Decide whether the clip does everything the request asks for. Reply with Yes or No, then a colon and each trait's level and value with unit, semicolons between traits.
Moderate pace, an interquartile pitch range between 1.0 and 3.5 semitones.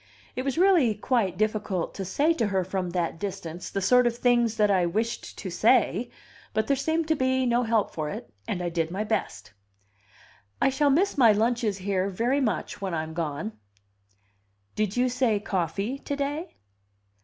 No: average, 180 wpm; average, 5.3 semitones